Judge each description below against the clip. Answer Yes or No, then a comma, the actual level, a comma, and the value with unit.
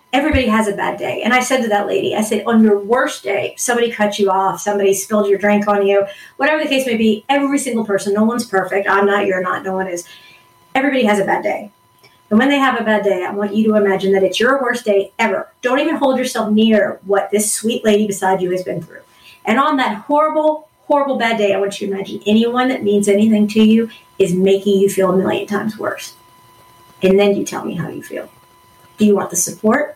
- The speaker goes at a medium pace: No, fast, 240 wpm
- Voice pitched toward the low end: No, high, 210 Hz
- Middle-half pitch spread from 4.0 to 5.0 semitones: No, average, 3.6 semitones